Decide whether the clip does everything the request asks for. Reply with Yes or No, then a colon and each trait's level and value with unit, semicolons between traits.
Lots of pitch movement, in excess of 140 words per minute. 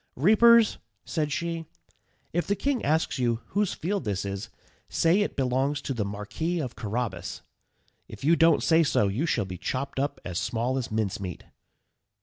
Yes: wide, 7.2 semitones; average, 165 wpm